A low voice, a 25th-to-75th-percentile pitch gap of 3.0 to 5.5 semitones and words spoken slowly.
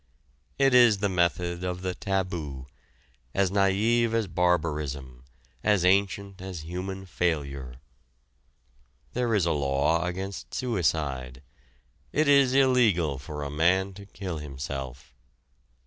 Yes: very low, 90 Hz; average, 5.0 semitones; slow, 115 wpm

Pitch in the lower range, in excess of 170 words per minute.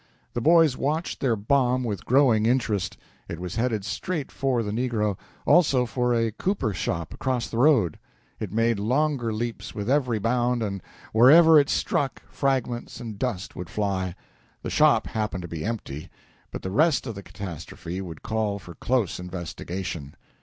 No: low, 115 Hz; average, 165 wpm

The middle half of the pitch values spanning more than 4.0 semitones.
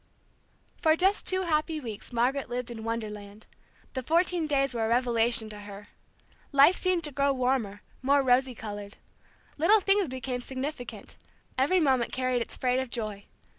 Yes: average, 4.5 semitones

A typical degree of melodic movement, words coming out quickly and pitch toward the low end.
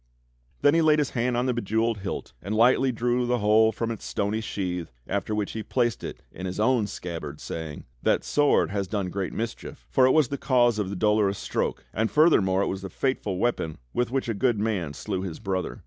Yes: average, 4.1 semitones; fast, 220 wpm; low, 110 Hz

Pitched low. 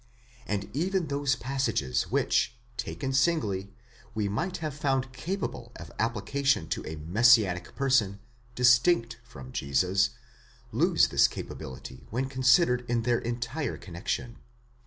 Yes: low, 120 Hz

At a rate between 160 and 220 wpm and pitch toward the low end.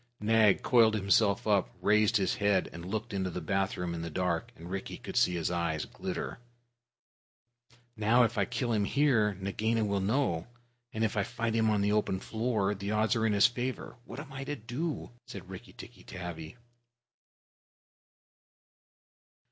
Yes: average, 170 wpm; low, 105 Hz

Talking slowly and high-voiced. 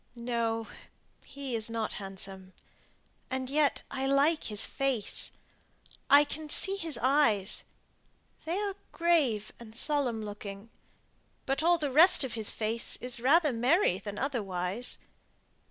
Yes: slow, 130 wpm; very high, 250 Hz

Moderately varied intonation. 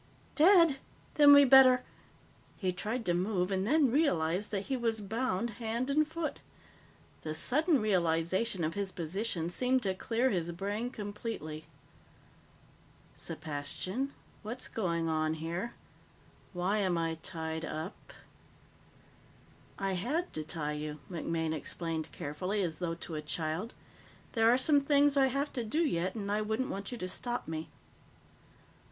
No: wide, 7.1 semitones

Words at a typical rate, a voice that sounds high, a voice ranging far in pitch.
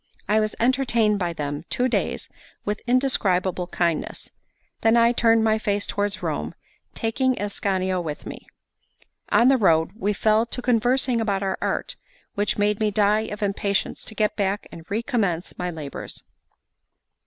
No: average, 155 wpm; high, 210 Hz; average, 3.3 semitones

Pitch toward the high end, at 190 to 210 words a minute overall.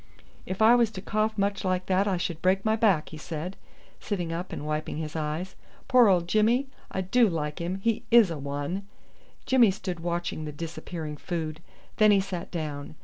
No: medium, 180 Hz; average, 195 wpm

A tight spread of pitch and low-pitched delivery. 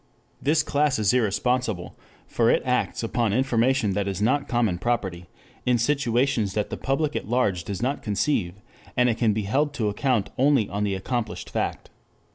No: average, 4.4 semitones; low, 120 Hz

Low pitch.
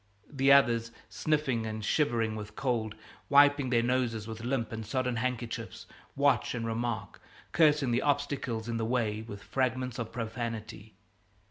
Yes: low, 120 Hz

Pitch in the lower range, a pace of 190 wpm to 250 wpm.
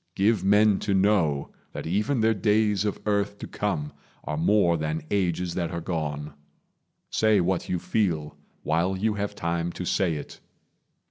No: very low, 95 Hz; average, 160 wpm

